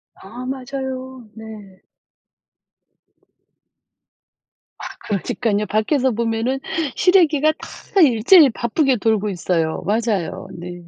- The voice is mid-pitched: No, high, 230 Hz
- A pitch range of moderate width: Yes, average, 4.5 semitones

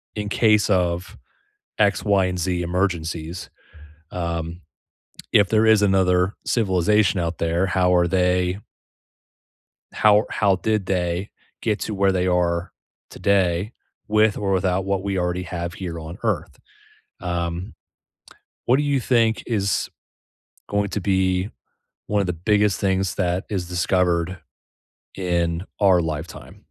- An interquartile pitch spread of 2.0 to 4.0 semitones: Yes, narrow, 2.6 semitones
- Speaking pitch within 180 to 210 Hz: No, very low, 95 Hz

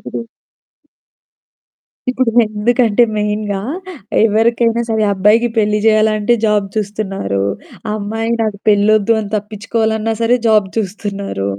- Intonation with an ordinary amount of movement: No, narrow, 1.5 semitones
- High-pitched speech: Yes, high, 215 Hz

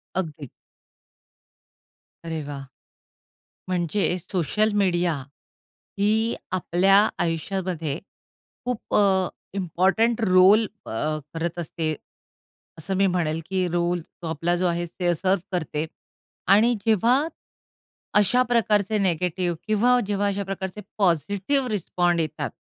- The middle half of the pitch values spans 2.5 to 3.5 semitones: Yes, average, 3.2 semitones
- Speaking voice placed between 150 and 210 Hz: Yes, medium, 185 Hz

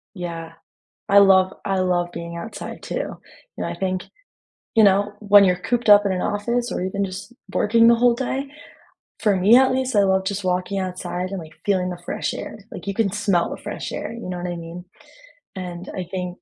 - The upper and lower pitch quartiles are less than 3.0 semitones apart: Yes, narrow, 2.4 semitones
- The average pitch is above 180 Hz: Yes, high, 190 Hz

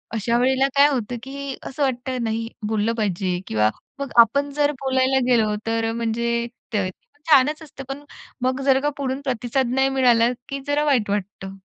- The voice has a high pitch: Yes, very high, 255 Hz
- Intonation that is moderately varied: Yes, average, 3.2 semitones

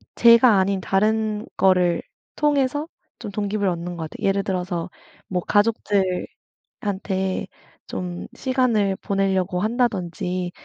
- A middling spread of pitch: Yes, average, 3.2 semitones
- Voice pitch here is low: No, high, 195 Hz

